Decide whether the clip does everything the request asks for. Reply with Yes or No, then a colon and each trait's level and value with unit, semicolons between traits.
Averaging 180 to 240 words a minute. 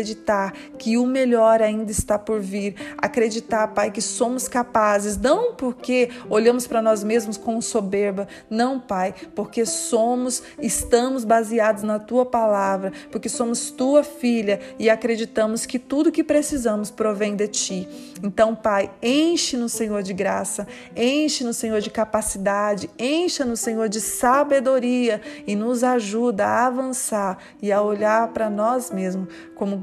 No: average, 145 wpm